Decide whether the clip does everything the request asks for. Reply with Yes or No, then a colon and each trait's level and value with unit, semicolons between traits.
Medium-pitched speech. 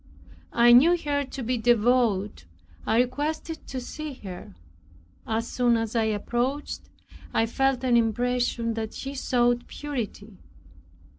No: high, 240 Hz